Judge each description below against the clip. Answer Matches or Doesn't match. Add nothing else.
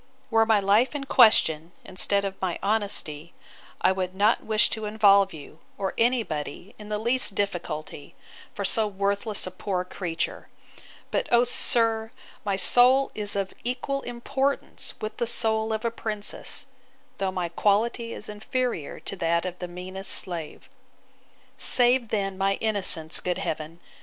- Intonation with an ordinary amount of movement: Matches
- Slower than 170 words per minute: Matches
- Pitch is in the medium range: Doesn't match